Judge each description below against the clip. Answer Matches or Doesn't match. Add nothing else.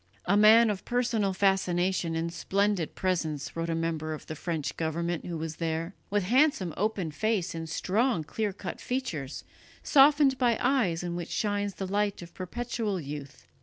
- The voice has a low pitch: Doesn't match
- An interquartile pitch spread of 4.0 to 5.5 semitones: Matches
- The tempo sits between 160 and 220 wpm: Matches